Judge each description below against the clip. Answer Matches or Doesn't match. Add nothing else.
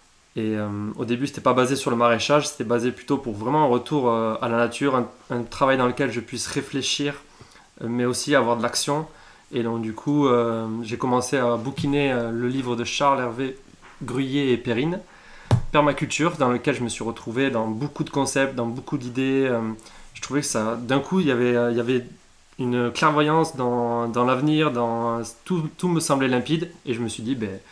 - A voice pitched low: Matches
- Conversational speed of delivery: Matches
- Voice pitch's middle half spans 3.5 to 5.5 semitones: Doesn't match